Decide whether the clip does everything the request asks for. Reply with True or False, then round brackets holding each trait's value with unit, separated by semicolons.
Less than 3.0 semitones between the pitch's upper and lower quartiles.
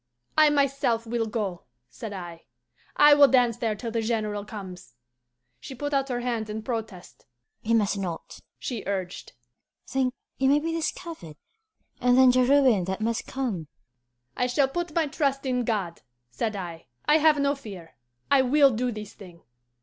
False (5.0 semitones)